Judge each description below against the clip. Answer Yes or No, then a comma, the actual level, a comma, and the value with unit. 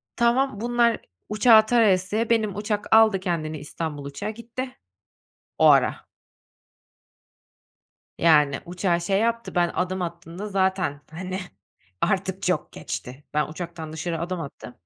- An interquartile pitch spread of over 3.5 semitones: Yes, average, 4.8 semitones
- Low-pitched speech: No, medium, 185 Hz